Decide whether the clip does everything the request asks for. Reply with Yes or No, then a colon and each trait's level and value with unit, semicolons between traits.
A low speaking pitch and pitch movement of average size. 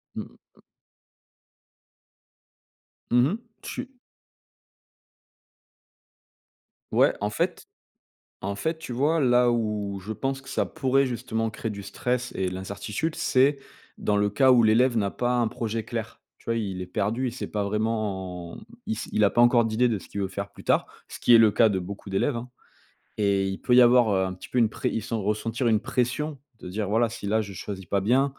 Yes: low, 110 Hz; average, 3.6 semitones